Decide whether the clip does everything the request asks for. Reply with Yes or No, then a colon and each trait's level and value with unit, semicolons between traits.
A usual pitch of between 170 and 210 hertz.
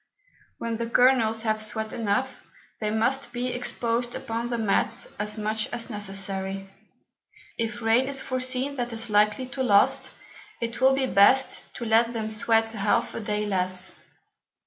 No: high, 225 Hz